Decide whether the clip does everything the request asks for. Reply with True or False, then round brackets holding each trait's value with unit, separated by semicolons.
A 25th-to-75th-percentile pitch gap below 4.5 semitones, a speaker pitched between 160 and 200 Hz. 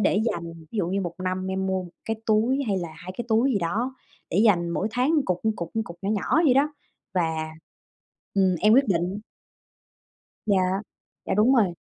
True (4.1 semitones; 190 Hz)